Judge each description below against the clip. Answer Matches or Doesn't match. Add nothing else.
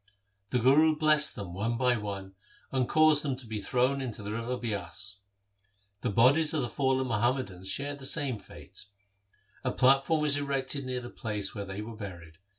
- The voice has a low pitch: Matches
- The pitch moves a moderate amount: Matches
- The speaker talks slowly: Doesn't match